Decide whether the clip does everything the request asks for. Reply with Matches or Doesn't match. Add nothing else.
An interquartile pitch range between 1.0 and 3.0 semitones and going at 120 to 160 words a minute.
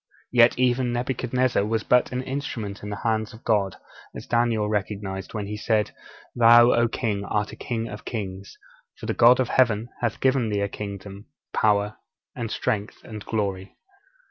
Doesn't match